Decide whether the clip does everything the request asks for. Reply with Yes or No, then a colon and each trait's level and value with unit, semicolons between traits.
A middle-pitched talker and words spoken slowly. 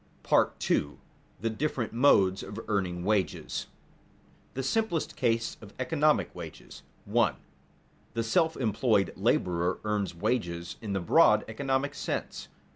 No: low, 110 Hz; slow, 125 wpm